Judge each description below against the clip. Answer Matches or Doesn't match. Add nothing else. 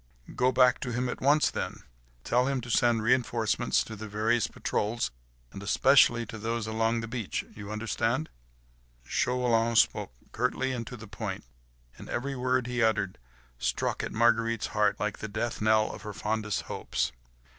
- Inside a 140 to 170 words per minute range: Matches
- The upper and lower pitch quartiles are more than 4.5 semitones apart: Doesn't match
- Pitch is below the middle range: Matches